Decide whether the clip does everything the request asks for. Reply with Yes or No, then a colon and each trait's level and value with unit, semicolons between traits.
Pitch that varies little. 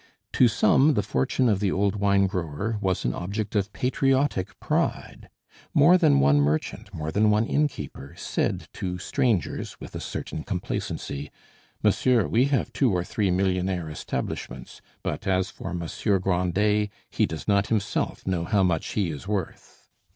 No: average, 3.4 semitones